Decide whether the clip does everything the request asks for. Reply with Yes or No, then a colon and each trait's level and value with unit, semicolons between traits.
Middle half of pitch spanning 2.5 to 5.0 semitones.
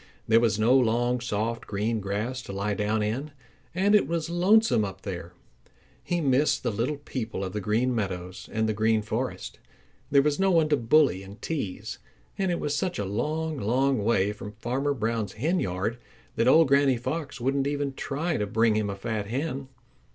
No: wide, 5.4 semitones